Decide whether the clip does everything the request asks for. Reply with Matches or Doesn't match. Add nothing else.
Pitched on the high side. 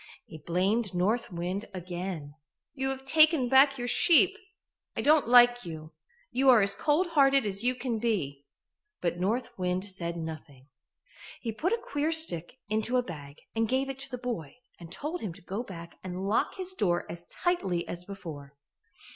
Matches